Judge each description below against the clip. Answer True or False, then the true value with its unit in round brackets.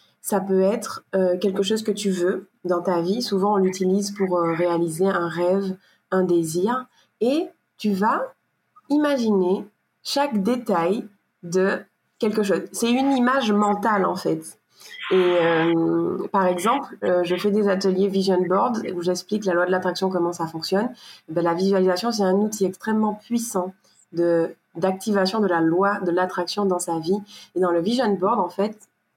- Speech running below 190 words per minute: True (170 wpm)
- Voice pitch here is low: False (190 Hz)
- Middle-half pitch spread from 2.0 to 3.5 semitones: True (2.8 semitones)